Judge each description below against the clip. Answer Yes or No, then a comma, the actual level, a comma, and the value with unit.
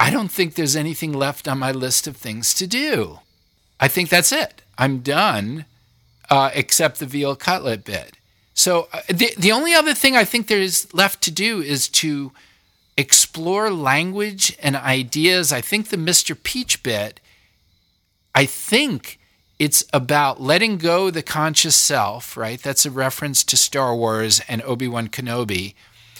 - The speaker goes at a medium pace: Yes, average, 160 wpm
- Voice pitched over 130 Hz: Yes, medium, 140 Hz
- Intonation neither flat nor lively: No, wide, 7.0 semitones